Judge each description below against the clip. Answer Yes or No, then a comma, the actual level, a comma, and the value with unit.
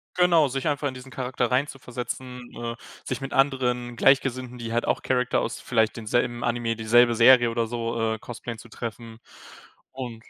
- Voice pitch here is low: Yes, low, 120 Hz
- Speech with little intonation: Yes, narrow, 1.8 semitones